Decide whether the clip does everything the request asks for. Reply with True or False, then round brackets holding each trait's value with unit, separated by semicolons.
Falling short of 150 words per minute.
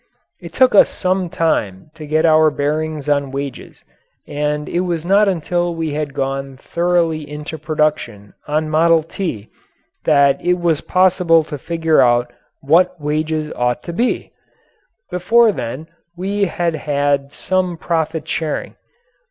True (140 wpm)